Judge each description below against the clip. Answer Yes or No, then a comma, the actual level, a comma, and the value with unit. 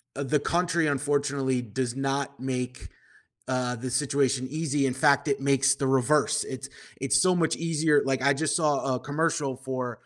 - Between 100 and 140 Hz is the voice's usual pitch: Yes, low, 135 Hz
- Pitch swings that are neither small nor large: No, narrow, 2.2 semitones